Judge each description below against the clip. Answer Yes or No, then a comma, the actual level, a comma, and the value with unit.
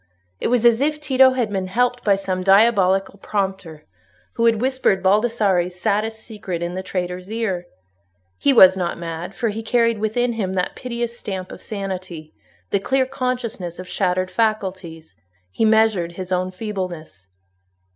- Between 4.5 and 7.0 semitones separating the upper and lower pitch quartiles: No, average, 4.0 semitones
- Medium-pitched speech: No, high, 195 Hz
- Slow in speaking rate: No, average, 155 wpm